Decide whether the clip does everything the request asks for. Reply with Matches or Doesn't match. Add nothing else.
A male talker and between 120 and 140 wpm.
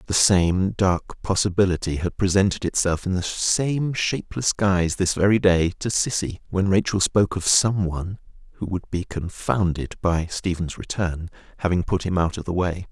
Doesn't match